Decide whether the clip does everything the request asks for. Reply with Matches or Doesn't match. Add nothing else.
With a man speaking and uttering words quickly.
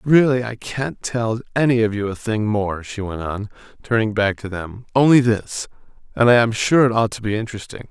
Matches